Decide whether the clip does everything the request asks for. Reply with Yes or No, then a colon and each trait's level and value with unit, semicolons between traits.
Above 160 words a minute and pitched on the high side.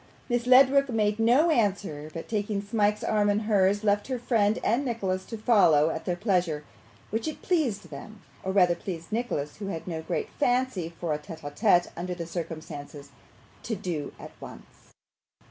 Yes: average, 180 wpm; high, 205 Hz